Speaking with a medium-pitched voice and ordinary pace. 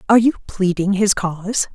No: high, 200 Hz; average, 170 wpm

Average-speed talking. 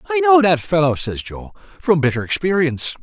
Yes: average, 180 wpm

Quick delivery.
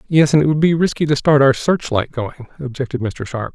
Yes: fast, 235 wpm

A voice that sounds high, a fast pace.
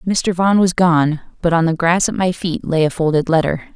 No: medium, 170 Hz; fast, 240 wpm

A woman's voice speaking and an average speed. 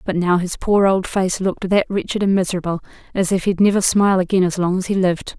No: female; fast, 245 wpm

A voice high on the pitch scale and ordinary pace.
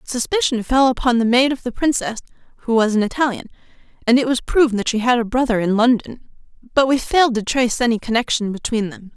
No: high, 240 Hz; fast, 210 wpm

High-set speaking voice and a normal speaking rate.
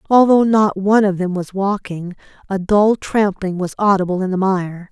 Yes: high, 195 Hz; average, 185 wpm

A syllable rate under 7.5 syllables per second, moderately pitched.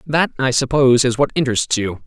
No: 6.1 syllables/s; low, 130 Hz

